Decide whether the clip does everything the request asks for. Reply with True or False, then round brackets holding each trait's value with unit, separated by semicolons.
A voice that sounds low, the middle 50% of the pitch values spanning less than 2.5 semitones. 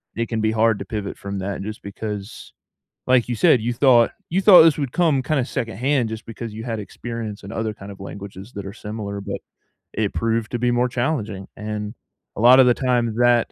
False (115 Hz; 2.8 semitones)